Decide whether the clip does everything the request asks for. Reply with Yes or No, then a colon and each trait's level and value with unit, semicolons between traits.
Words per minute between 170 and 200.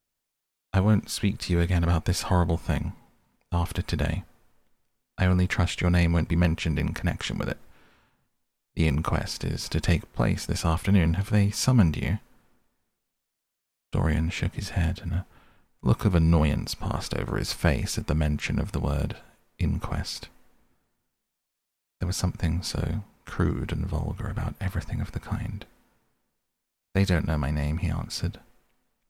No: average, 155 wpm